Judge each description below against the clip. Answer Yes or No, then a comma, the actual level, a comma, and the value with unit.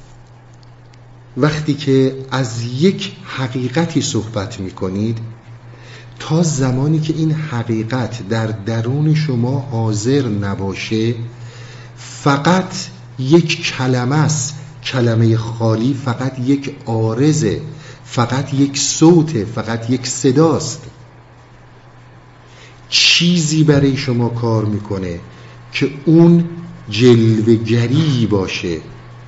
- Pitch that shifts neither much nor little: Yes, average, 3.5 semitones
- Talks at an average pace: No, slow, 85 wpm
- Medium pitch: No, low, 125 Hz